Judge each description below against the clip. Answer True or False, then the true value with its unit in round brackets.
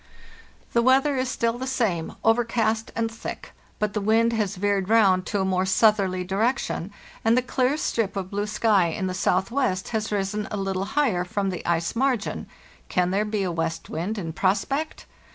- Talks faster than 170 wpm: True (190 wpm)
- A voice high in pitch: True (210 Hz)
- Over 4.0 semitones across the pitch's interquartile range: False (3.5 semitones)